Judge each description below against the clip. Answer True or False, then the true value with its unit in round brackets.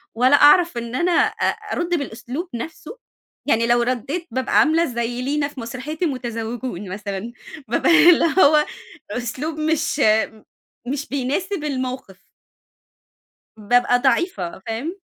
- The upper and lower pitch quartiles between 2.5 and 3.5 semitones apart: False (4.9 semitones)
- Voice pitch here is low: False (260 Hz)